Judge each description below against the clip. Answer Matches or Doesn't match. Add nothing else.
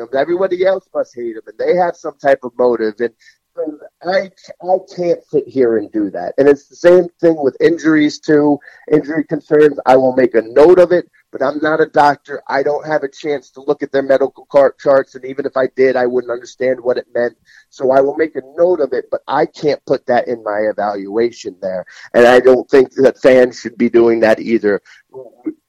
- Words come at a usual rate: Doesn't match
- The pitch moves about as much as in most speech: Doesn't match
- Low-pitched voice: Doesn't match